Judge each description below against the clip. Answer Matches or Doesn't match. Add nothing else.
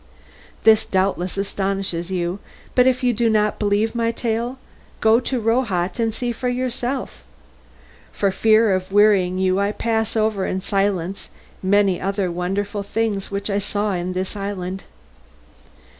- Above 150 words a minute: Doesn't match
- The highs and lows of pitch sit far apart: Doesn't match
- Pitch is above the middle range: Matches